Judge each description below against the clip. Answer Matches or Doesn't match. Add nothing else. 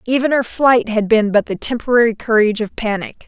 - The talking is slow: Doesn't match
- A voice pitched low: Doesn't match